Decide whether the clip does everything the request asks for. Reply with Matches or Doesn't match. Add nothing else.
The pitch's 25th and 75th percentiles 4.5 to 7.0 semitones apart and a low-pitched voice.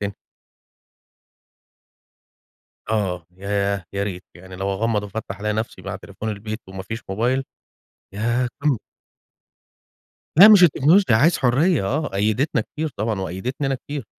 Matches